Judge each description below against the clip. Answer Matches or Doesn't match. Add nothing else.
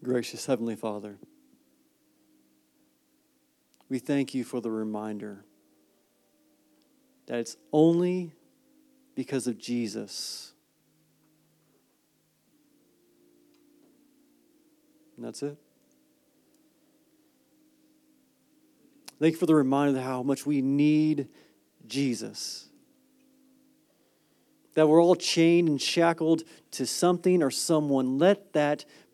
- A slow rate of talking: Matches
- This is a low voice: Doesn't match